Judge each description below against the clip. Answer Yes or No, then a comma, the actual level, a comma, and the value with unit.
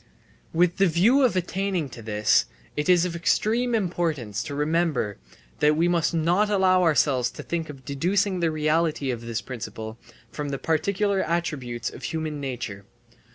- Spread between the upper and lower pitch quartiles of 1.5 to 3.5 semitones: No, average, 4.9 semitones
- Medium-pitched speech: Yes, medium, 160 Hz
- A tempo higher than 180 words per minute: No, average, 160 wpm